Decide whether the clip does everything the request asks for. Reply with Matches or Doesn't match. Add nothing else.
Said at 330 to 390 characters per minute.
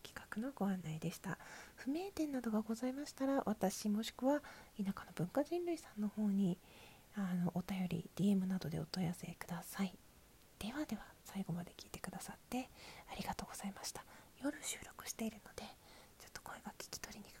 Matches